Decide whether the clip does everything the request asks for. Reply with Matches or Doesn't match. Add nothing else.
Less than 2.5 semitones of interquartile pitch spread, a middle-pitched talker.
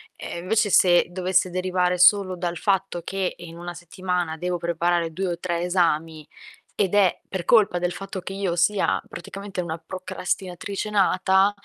Matches